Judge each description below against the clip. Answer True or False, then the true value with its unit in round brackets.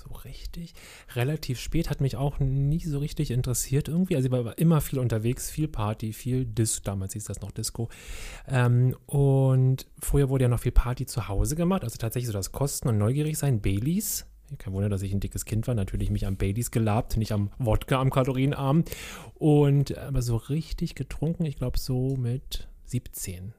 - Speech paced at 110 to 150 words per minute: False (190 wpm)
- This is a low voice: True (125 Hz)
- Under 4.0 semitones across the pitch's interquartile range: False (4.3 semitones)